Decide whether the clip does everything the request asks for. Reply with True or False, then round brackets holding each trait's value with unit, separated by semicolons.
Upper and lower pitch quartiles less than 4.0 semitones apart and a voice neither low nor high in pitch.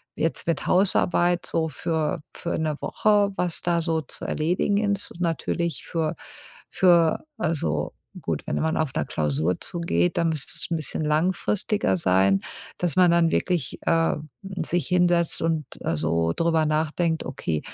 True (2.6 semitones; 165 Hz)